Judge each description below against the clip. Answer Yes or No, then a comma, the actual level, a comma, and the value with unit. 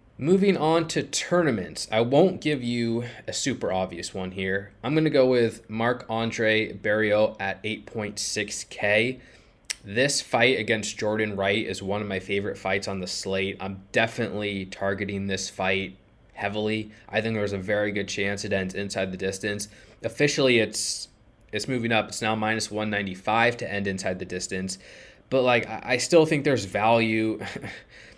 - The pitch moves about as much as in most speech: Yes, average, 3.0 semitones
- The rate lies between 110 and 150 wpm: No, average, 160 wpm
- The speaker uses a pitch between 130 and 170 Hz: No, low, 105 Hz